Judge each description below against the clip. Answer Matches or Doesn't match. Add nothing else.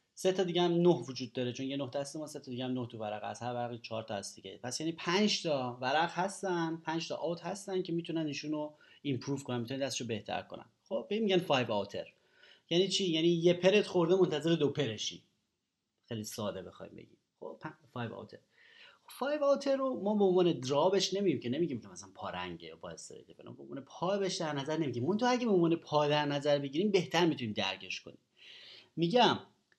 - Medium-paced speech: Doesn't match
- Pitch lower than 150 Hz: Doesn't match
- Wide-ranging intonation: Matches